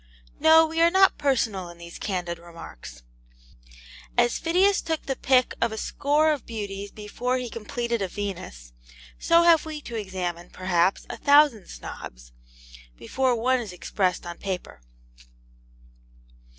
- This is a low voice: No, high, 220 Hz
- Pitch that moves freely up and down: Yes, wide, 7.9 semitones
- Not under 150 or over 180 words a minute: No, average, 140 wpm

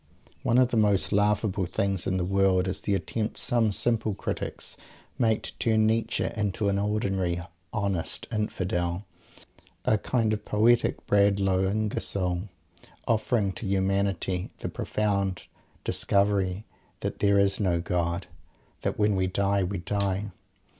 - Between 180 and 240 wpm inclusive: No, average, 140 wpm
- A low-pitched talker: Yes, low, 100 Hz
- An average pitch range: No, narrow, 2.1 semitones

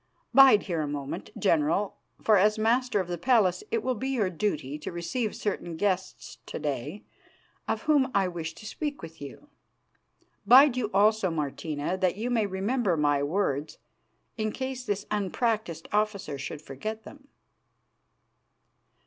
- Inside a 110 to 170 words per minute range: Yes, average, 150 wpm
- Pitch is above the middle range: Yes, high, 200 Hz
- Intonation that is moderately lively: No, wide, 6.0 semitones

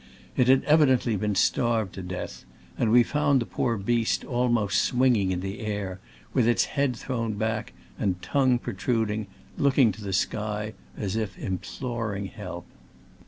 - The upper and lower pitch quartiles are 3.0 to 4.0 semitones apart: Yes, average, 3.4 semitones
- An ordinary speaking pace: Yes, average, 160 wpm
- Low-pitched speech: Yes, low, 110 Hz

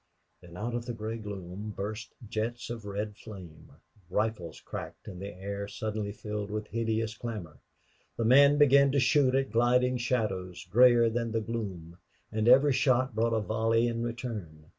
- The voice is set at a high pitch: No, low, 110 Hz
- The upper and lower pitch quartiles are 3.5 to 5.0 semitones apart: No, average, 2.8 semitones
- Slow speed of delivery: No, average, 165 wpm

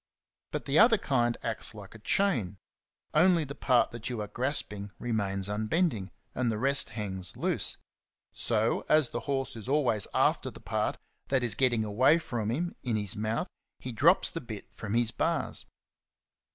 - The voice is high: No, low, 120 Hz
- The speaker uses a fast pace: No, average, 175 wpm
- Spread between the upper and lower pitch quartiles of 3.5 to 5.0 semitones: Yes, average, 4.6 semitones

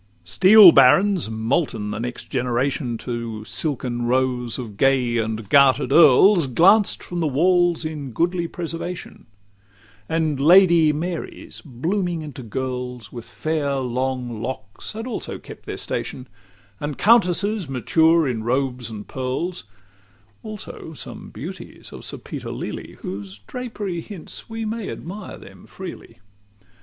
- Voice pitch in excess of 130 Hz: Yes, medium, 140 Hz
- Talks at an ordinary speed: No, slow, 130 wpm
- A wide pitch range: Yes, wide, 6.2 semitones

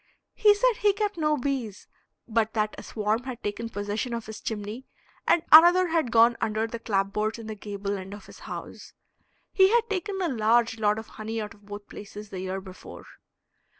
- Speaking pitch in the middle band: No, high, 225 Hz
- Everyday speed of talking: Yes, average, 195 wpm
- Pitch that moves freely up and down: Yes, wide, 6.4 semitones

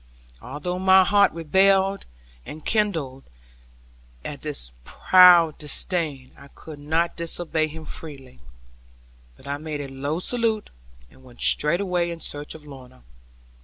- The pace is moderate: No, slow, 125 wpm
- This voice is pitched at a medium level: Yes, medium, 160 Hz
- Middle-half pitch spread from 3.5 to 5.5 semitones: Yes, average, 4.1 semitones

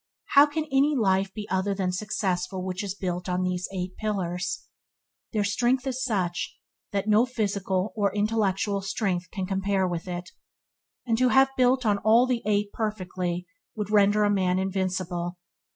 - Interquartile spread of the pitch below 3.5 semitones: Yes, average, 2.9 semitones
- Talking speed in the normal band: Yes, average, 160 wpm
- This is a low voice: No, high, 200 Hz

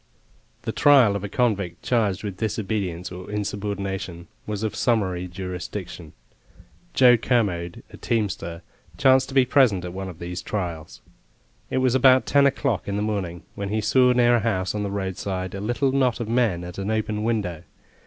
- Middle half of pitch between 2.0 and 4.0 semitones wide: No, average, 4.4 semitones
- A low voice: Yes, low, 100 Hz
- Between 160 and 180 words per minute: Yes, average, 175 wpm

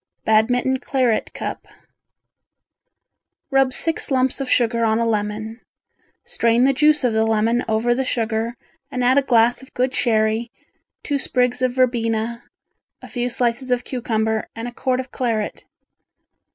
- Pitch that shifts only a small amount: Yes, narrow, 2.3 semitones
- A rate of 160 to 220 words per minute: No, average, 150 wpm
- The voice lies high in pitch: Yes, high, 240 Hz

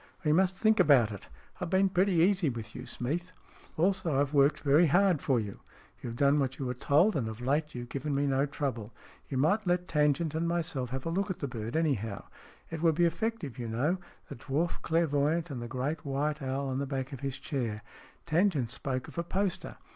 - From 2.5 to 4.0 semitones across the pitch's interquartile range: No, average, 4.5 semitones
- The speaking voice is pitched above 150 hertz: No, medium, 145 Hz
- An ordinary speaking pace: No, fast, 220 wpm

